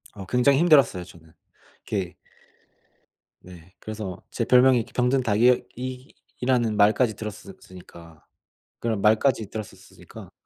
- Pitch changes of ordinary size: Yes, average, 4.7 semitones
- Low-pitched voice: Yes, low, 110 Hz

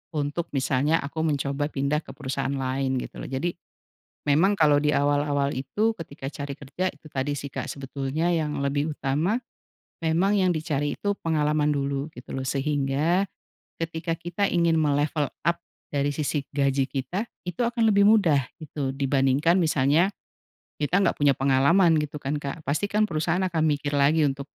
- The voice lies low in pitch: No, medium, 150 Hz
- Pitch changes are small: No, average, 3.0 semitones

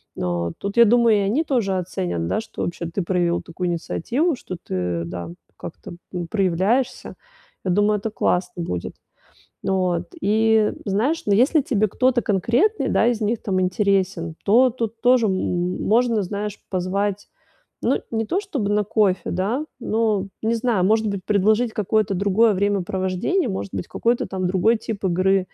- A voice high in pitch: Yes, high, 200 Hz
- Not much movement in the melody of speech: No, average, 3.7 semitones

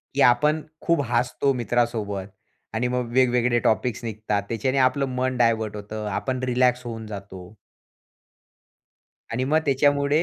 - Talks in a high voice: No, low, 120 Hz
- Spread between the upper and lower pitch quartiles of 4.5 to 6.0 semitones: No, average, 2.7 semitones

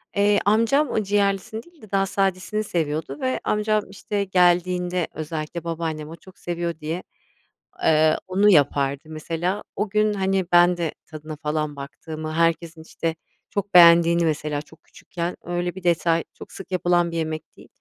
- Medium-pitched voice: Yes, medium, 175 Hz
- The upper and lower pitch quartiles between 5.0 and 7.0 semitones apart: No, average, 3.5 semitones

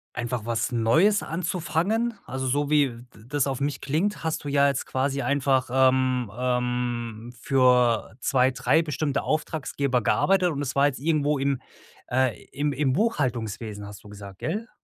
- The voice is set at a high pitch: No, low, 135 Hz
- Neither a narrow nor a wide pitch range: Yes, average, 3.2 semitones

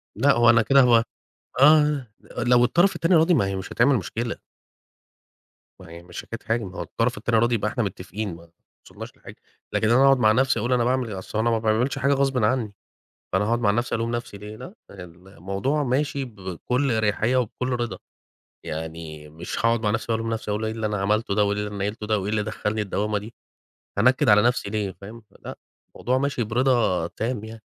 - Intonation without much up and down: No, average, 3.2 semitones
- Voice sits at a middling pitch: No, low, 110 Hz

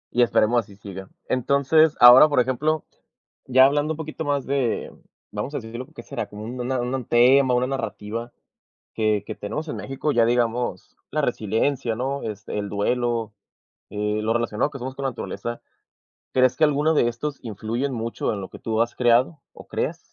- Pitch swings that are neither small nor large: Yes, average, 3.5 semitones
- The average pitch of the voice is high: No, low, 120 Hz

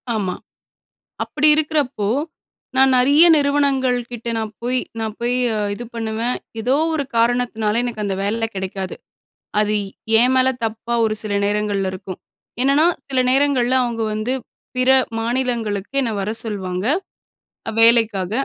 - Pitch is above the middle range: Yes, high, 230 Hz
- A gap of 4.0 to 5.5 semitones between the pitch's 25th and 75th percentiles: No, average, 3.5 semitones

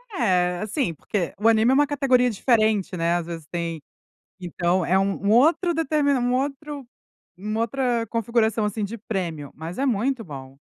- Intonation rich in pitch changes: Yes, wide, 6.3 semitones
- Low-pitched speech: No, high, 220 Hz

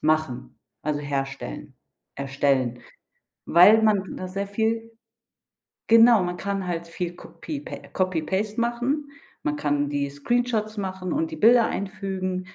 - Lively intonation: Yes, wide, 6.4 semitones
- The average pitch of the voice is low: No, high, 190 Hz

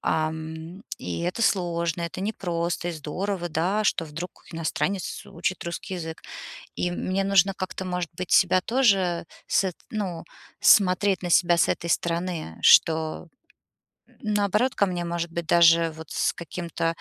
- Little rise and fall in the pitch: Yes, narrow, 2.2 semitones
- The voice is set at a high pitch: No, medium, 175 Hz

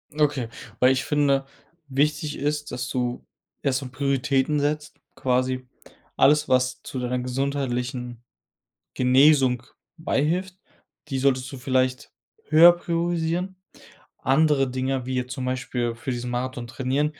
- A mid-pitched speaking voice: No, low, 130 Hz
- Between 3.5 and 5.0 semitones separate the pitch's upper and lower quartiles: No, average, 2.7 semitones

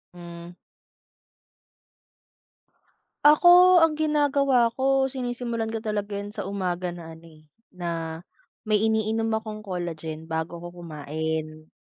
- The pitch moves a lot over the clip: Yes, wide, 6.5 semitones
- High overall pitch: Yes, high, 200 Hz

